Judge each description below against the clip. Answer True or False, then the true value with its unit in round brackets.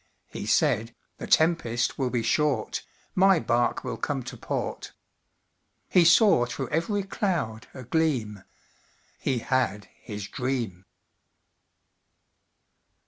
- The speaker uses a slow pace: True (110 wpm)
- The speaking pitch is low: True (130 Hz)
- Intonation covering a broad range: True (6.1 semitones)